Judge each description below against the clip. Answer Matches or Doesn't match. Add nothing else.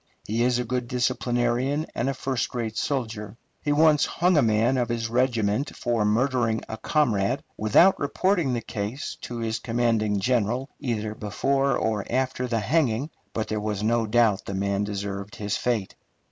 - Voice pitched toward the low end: Matches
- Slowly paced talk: Doesn't match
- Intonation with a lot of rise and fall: Doesn't match